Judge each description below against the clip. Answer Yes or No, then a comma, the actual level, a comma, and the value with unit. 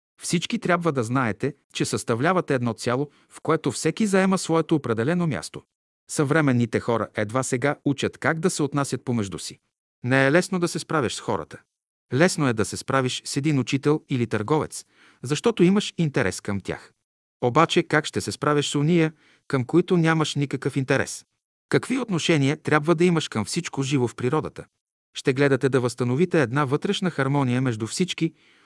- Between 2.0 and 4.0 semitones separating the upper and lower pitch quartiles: No, average, 4.5 semitones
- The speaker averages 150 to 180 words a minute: Yes, fast, 165 wpm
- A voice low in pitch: No, medium, 145 Hz